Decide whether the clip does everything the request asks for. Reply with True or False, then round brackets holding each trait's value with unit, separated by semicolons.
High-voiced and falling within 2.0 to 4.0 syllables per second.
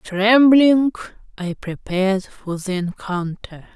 True (205 Hz; 3.7 syllables/s)